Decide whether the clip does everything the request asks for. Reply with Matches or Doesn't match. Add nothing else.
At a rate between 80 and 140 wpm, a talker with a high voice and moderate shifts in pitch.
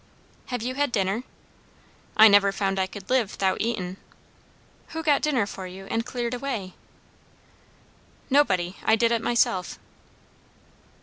Matches